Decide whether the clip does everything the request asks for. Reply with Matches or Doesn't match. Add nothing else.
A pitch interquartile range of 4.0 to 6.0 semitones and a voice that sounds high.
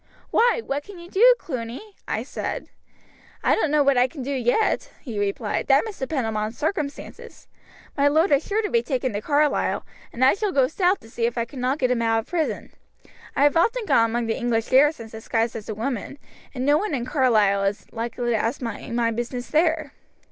Matches